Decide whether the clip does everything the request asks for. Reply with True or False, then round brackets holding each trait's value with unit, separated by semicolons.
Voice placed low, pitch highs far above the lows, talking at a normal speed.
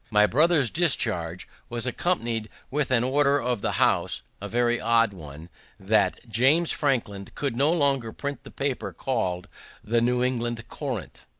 False (120 Hz; 4.2 semitones; 155 wpm)